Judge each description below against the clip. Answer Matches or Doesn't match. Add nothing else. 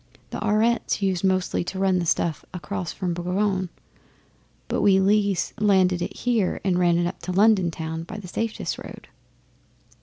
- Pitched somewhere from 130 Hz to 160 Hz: Doesn't match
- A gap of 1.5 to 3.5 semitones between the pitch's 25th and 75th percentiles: Matches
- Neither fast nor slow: Matches